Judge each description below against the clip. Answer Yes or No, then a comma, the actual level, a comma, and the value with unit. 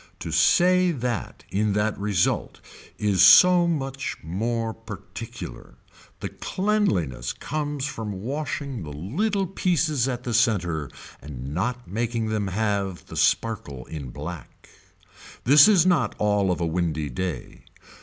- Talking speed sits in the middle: No, slow, 130 wpm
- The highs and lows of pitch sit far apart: Yes, wide, 7.8 semitones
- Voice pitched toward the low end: Yes, low, 110 Hz